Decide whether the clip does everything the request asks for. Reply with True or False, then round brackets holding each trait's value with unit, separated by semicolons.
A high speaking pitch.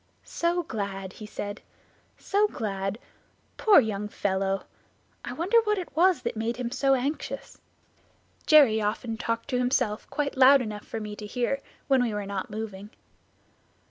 True (230 Hz)